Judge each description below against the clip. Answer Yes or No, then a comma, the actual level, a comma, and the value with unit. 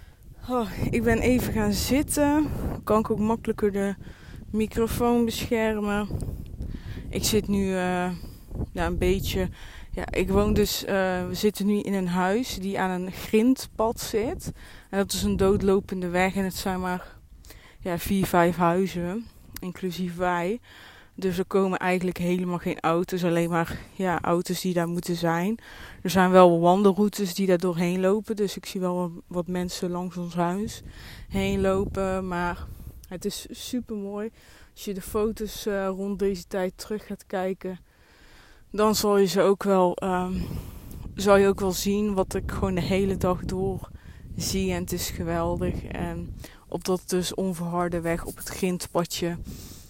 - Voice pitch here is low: No, high, 190 Hz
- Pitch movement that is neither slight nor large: No, narrow, 2.3 semitones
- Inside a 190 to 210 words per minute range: No, average, 165 wpm